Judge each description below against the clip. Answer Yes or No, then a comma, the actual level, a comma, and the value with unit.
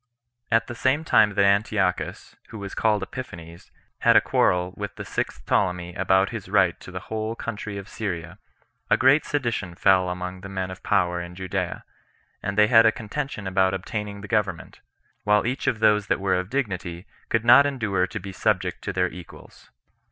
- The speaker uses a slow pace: No, average, 190 wpm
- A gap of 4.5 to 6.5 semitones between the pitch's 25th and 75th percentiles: No, average, 3.1 semitones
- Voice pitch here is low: Yes, low, 100 Hz